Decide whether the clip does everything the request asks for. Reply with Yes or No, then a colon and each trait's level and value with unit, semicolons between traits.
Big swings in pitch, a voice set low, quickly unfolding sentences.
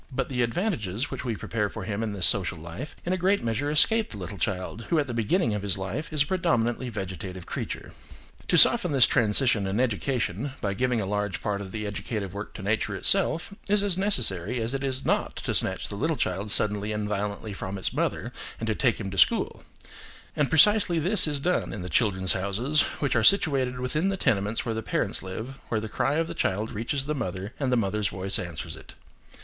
Yes: wide, 5.8 semitones; low, 115 Hz; fast, 220 wpm